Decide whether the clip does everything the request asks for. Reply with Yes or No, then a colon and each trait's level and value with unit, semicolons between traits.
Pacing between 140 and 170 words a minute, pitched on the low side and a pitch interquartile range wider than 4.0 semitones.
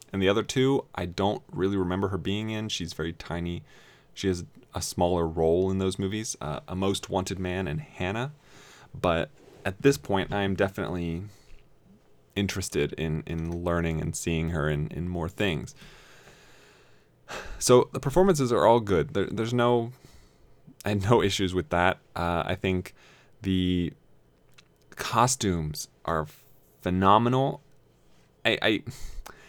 Yes: average, 145 wpm; very low, 95 Hz; average, 4.7 semitones